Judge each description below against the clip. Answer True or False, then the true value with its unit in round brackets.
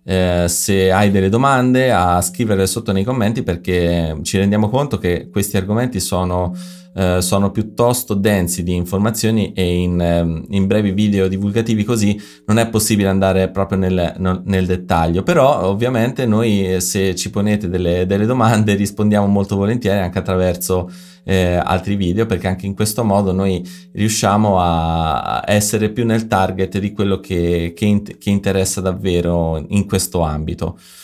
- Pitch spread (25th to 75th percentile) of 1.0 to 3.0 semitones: True (2.7 semitones)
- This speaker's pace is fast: False (150 wpm)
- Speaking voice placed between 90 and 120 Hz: True (95 Hz)